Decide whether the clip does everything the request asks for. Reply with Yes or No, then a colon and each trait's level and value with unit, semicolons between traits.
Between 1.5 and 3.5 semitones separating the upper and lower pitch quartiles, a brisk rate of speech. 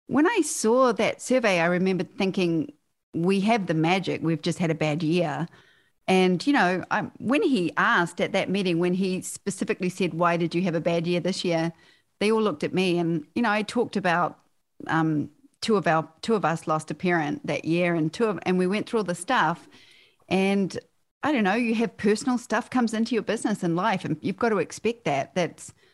No: average, 4.5 semitones; fast, 220 wpm